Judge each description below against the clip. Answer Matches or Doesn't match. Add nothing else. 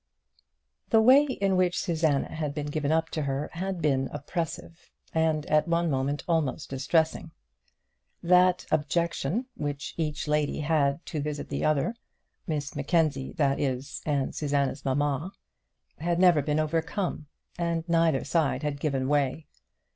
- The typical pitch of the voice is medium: Matches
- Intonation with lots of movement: Doesn't match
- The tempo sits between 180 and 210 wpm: Doesn't match